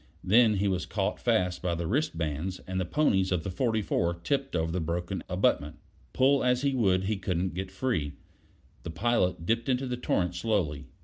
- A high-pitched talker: No, very low, 95 Hz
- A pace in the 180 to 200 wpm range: Yes, average, 185 wpm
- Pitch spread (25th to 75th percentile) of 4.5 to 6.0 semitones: Yes, wide, 5.4 semitones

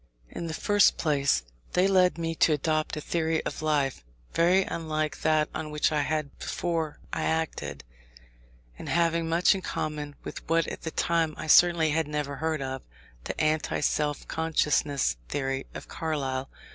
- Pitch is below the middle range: No, medium, 155 Hz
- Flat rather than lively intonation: Yes, narrow, 2.0 semitones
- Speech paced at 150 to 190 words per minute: Yes, average, 165 wpm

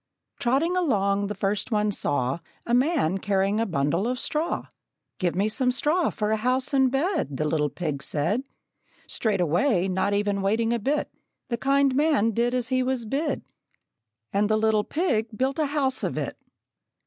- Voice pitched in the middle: No, high, 225 Hz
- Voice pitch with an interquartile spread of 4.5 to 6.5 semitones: Yes, average, 5.2 semitones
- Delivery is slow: No, average, 175 wpm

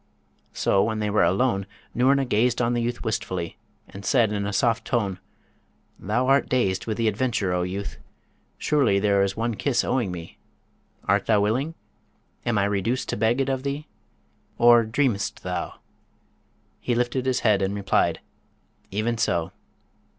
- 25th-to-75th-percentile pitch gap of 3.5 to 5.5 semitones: Yes, average, 3.8 semitones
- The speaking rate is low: No, average, 160 wpm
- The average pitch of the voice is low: Yes, low, 110 Hz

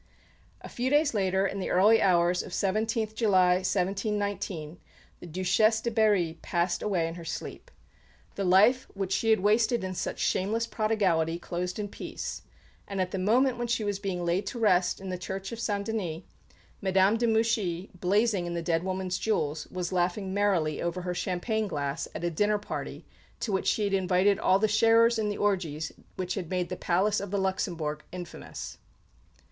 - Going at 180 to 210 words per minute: Yes, average, 185 wpm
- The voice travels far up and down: No, average, 3.1 semitones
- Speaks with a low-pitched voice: No, high, 190 Hz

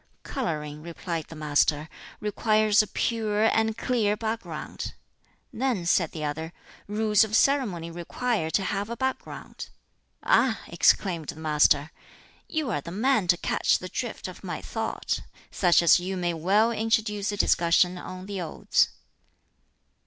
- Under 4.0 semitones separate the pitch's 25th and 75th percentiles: No, average, 4.7 semitones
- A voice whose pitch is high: Yes, high, 195 Hz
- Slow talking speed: No, average, 145 wpm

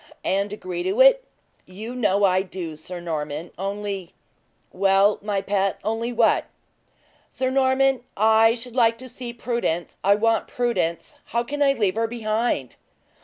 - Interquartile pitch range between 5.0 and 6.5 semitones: No, average, 4.0 semitones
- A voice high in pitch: Yes, high, 215 Hz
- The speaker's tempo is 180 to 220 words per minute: No, average, 155 wpm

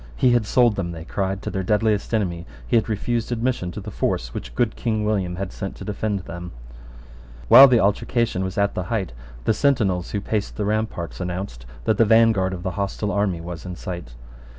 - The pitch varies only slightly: No, average, 3.6 semitones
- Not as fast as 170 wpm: No, fast, 205 wpm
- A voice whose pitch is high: No, low, 100 Hz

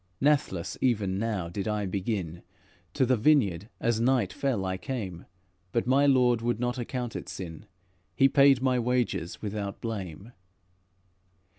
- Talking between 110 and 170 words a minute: Yes, average, 145 wpm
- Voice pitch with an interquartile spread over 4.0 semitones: Yes, average, 4.9 semitones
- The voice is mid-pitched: No, low, 115 Hz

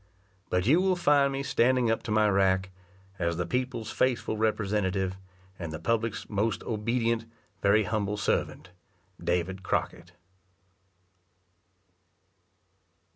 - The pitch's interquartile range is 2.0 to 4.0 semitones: Yes, average, 3.7 semitones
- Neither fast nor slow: No, slow, 115 wpm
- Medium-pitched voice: No, low, 105 Hz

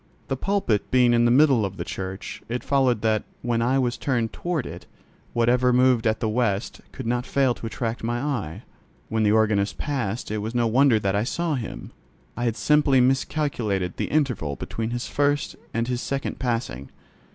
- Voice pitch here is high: No, low, 120 Hz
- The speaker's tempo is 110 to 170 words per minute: No, average, 195 wpm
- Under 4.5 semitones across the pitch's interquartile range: Yes, average, 3.3 semitones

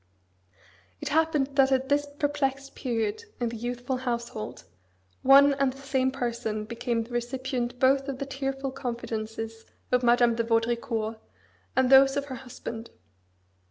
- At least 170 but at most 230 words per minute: No, average, 145 wpm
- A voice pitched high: Yes, very high, 255 Hz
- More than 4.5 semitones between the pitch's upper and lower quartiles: No, narrow, 2.5 semitones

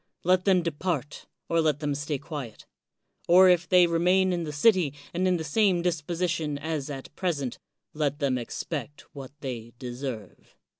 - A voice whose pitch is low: No, medium, 155 Hz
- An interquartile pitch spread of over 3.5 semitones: Yes, average, 3.9 semitones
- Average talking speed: Yes, average, 160 wpm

